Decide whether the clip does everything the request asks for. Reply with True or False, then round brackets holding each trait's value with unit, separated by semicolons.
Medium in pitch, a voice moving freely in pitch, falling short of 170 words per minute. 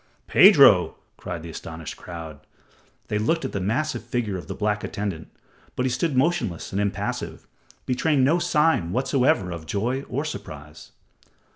False (105 Hz; 7.6 semitones; 150 wpm)